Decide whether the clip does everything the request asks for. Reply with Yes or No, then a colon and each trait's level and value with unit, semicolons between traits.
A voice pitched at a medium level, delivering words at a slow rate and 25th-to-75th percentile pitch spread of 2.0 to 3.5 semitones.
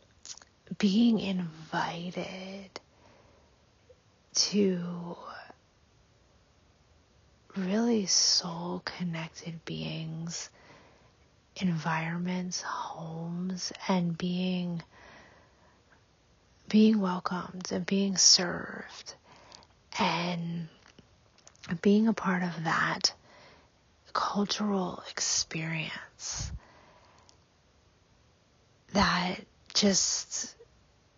Yes: medium, 180 Hz; slow, 50 wpm; average, 2.7 semitones